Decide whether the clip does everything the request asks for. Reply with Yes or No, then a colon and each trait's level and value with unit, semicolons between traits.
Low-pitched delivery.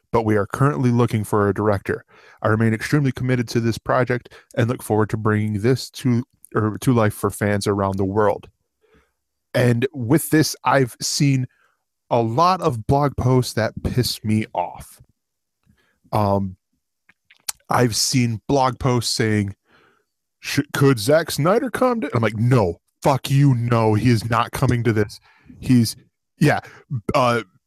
Yes: low, 120 Hz